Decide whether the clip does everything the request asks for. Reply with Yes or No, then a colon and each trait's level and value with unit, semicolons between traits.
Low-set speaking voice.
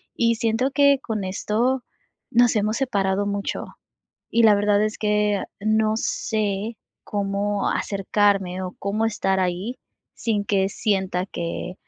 No: high, 205 Hz